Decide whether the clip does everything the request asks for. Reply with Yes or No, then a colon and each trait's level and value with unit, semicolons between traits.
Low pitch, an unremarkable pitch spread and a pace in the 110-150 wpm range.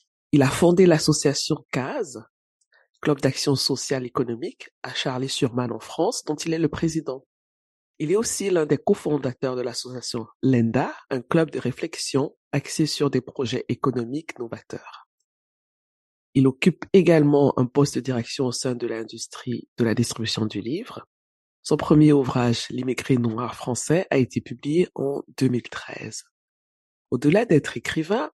Yes: low, 130 Hz; average, 3.7 semitones; slow, 145 wpm